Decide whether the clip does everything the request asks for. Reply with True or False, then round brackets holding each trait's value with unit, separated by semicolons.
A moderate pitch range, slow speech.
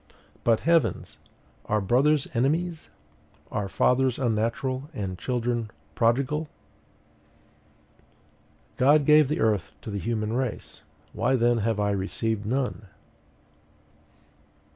True (4.0 semitones; 100 wpm)